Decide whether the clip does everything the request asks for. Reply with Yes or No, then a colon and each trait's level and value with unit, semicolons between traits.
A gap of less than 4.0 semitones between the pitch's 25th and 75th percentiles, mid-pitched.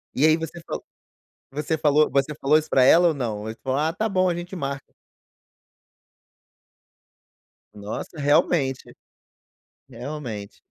Yes: average, 3.5 semitones; medium, 150 Hz